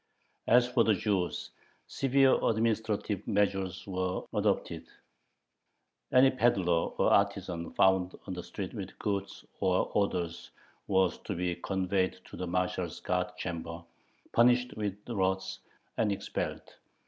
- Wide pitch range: No, average, 3.2 semitones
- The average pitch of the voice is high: No, very low, 95 Hz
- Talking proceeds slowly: Yes, slow, 125 wpm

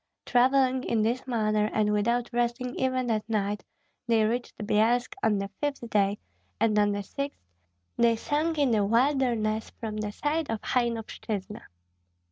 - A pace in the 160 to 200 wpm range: No, average, 150 wpm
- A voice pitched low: No, high, 230 Hz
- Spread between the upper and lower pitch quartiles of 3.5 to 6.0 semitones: No, average, 3.0 semitones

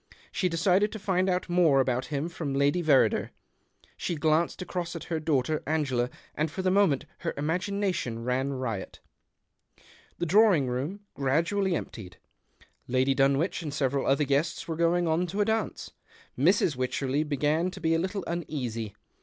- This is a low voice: No, medium, 155 Hz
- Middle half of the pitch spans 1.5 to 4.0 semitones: No, average, 4.7 semitones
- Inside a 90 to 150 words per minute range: No, average, 160 wpm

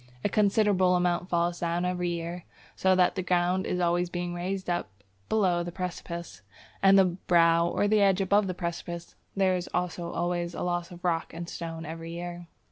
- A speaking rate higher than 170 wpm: Yes, average, 185 wpm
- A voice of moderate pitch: Yes, medium, 175 Hz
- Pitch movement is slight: Yes, narrow, 1.2 semitones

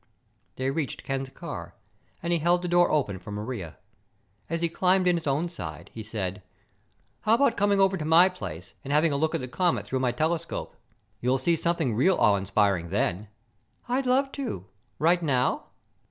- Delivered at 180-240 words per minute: Yes, average, 185 wpm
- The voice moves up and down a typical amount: No, wide, 8.2 semitones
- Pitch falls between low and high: Yes, medium, 150 Hz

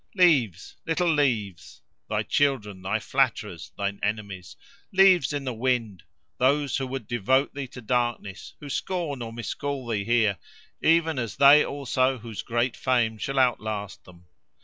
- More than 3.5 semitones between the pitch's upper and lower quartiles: Yes, average, 4.7 semitones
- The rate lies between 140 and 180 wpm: Yes, average, 150 wpm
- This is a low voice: Yes, low, 125 Hz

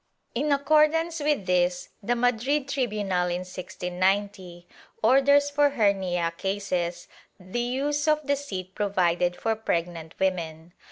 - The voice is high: Yes, high, 200 Hz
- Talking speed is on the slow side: Yes, slow, 125 wpm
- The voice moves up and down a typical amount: No, wide, 7.7 semitones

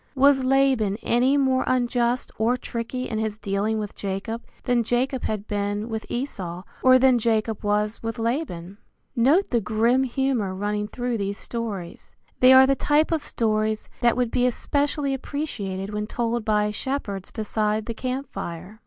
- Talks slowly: No, average, 160 wpm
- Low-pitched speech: No, high, 230 Hz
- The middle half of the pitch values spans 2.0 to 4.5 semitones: Yes, average, 3.6 semitones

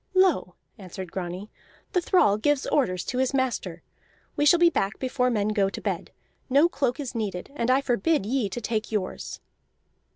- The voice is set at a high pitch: Yes, high, 240 Hz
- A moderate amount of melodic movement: No, wide, 5.8 semitones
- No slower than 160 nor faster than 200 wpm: Yes, average, 175 wpm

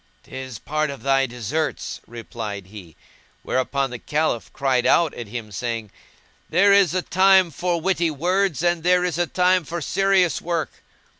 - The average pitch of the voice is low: No, medium, 155 Hz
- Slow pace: No, average, 155 wpm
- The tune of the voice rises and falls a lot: Yes, wide, 6.5 semitones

